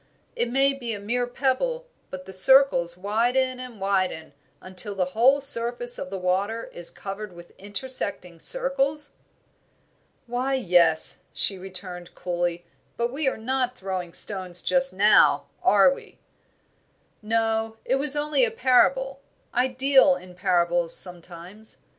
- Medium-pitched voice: No, high, 220 Hz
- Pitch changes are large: Yes, wide, 6.2 semitones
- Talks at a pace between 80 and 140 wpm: Yes, slow, 135 wpm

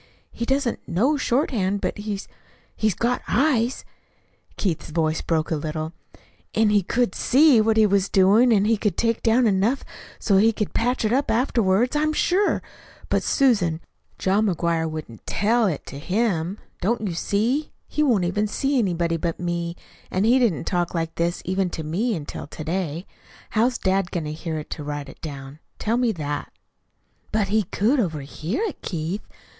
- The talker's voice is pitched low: No, high, 200 Hz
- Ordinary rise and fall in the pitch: No, wide, 5.8 semitones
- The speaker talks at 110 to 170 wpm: No, average, 180 wpm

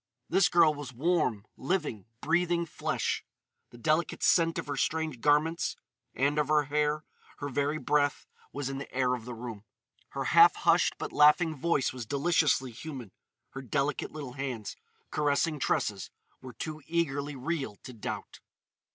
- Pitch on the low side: No, medium, 145 Hz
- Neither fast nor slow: Yes, average, 155 wpm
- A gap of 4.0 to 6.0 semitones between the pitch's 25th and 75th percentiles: No, average, 3.3 semitones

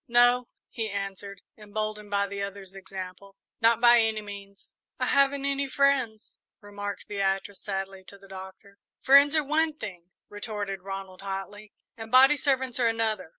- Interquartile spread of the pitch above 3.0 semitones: Yes, average, 3.7 semitones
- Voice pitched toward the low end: No, high, 205 Hz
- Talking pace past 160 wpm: No, average, 150 wpm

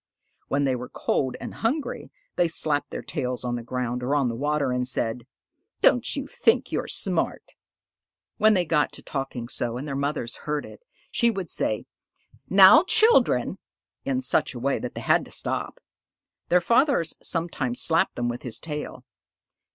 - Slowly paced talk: No, average, 175 wpm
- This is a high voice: No, medium, 140 Hz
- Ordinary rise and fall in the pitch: No, wide, 5.9 semitones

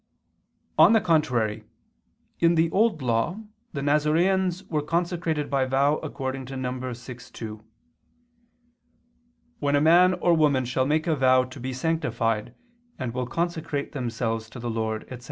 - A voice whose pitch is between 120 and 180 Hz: Yes, low, 135 Hz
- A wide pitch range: No, average, 4.6 semitones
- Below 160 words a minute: Yes, average, 145 wpm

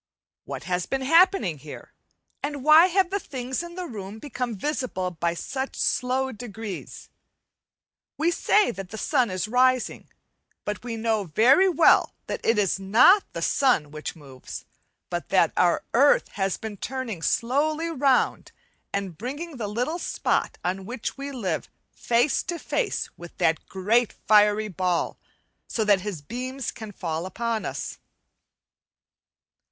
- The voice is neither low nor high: No, high, 230 Hz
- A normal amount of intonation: No, wide, 6.2 semitones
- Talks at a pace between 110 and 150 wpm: Yes, average, 145 wpm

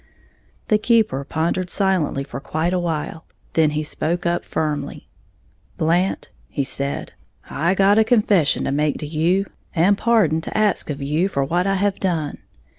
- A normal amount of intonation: Yes, average, 4.3 semitones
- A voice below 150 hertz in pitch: No, medium, 170 Hz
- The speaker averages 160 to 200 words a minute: Yes, average, 165 wpm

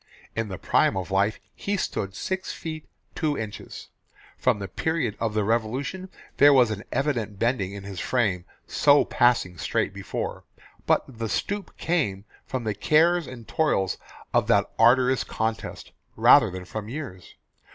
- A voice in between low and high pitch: No, low, 115 Hz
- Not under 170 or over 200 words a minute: No, average, 155 wpm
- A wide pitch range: Yes, wide, 6.2 semitones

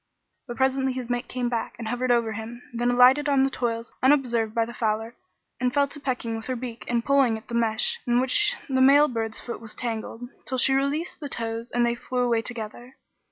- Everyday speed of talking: No, fast, 220 wpm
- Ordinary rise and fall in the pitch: No, narrow, 2.2 semitones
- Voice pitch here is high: Yes, high, 245 Hz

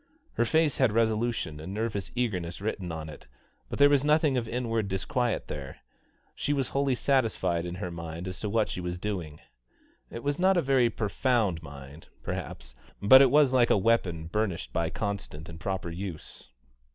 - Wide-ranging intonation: Yes, wide, 6.6 semitones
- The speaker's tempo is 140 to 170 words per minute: No, average, 185 wpm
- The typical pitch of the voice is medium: No, low, 105 Hz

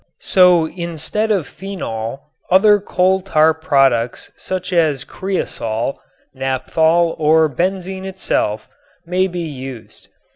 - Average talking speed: No, slow, 105 wpm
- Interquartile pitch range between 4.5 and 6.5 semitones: Yes, wide, 5.5 semitones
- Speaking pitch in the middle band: Yes, medium, 165 Hz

